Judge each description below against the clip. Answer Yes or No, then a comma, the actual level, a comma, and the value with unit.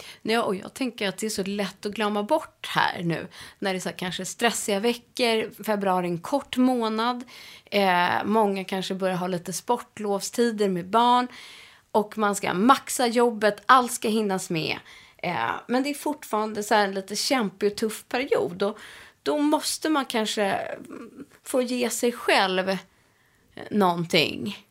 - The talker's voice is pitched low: No, high, 215 Hz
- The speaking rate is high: No, average, 165 wpm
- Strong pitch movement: No, average, 3.8 semitones